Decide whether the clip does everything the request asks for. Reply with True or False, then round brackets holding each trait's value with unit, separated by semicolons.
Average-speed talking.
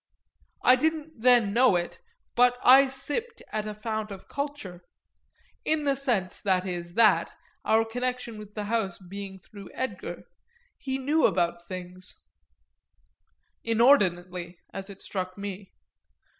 False (130 wpm)